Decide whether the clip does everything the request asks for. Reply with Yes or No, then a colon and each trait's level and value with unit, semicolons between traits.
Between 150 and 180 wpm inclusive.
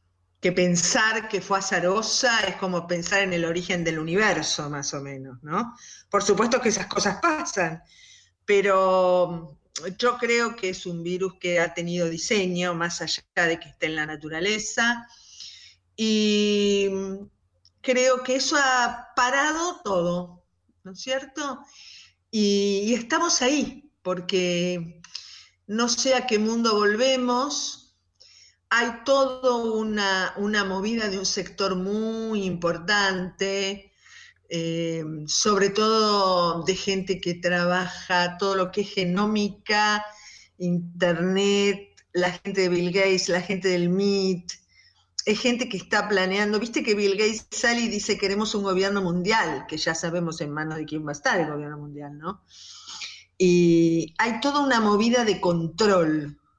No: average, 140 wpm